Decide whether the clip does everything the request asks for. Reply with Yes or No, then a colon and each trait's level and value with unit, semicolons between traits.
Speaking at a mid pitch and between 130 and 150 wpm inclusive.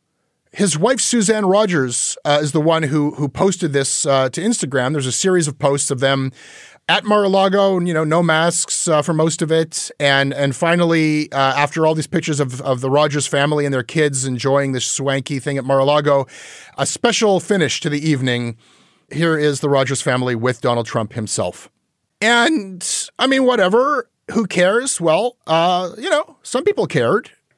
No: medium, 150 Hz; average, 180 wpm